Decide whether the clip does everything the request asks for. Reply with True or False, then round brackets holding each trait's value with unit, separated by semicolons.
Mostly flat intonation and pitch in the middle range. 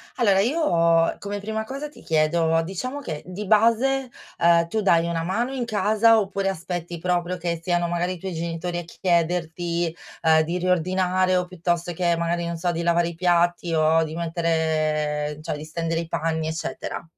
True (2.3 semitones; 175 Hz)